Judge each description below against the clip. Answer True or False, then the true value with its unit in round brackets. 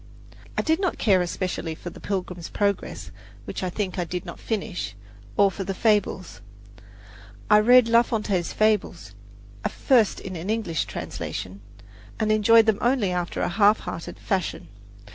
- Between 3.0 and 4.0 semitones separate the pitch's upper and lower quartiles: True (3.6 semitones)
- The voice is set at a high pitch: True (200 Hz)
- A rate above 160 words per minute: False (155 wpm)